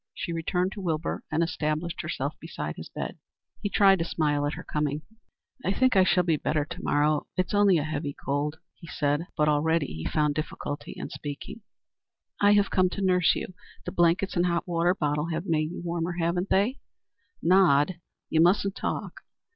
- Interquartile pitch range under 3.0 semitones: No, average, 3.4 semitones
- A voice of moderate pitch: Yes, medium, 170 Hz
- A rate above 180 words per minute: Yes, average, 190 wpm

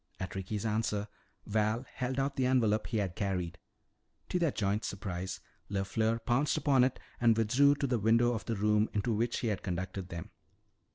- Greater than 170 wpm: Yes, average, 180 wpm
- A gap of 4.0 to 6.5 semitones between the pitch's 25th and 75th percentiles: No, average, 3.6 semitones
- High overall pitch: No, low, 110 Hz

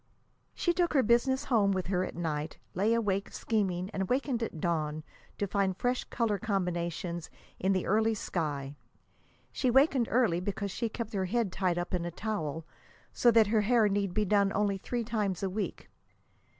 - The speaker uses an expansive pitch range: No, average, 4.2 semitones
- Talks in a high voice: Yes, high, 200 Hz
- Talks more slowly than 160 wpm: No, average, 180 wpm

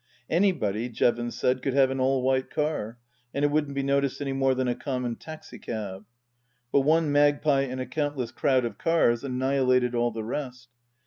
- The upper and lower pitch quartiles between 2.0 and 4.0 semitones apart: Yes, average, 2.7 semitones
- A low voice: Yes, low, 130 Hz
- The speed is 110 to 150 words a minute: No, average, 185 wpm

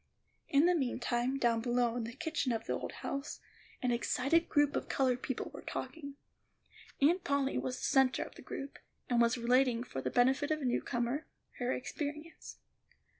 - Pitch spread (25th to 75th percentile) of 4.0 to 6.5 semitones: No, average, 2.9 semitones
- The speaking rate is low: No, average, 180 wpm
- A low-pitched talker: No, very high, 260 Hz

